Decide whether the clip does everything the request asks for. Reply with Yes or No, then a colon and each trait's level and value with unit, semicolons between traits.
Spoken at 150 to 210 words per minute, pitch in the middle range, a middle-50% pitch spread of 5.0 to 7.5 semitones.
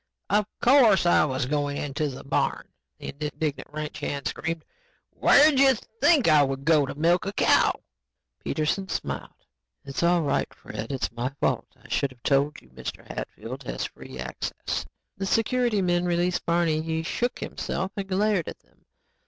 Yes: average, 170 wpm; medium, 160 Hz; wide, 5.4 semitones